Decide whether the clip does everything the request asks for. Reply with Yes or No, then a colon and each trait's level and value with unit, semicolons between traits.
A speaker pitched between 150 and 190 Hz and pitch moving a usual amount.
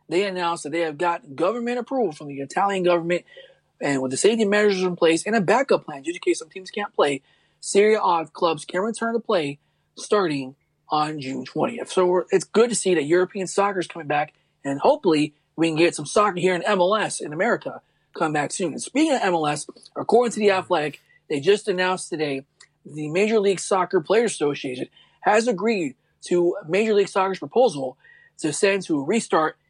Yes: medium, 185 Hz; average, 5.0 semitones